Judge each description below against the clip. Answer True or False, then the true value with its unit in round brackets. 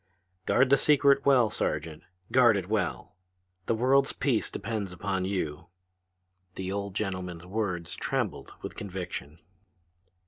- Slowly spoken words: True (125 wpm)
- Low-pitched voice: True (100 Hz)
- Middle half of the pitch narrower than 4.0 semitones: False (5.2 semitones)